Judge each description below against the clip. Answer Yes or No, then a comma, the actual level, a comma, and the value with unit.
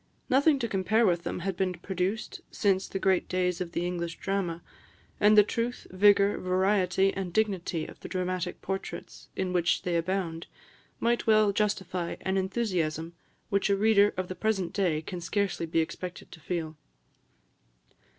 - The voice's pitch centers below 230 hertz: Yes, medium, 185 Hz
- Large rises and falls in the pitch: No, narrow, 2.4 semitones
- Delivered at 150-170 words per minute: Yes, average, 160 wpm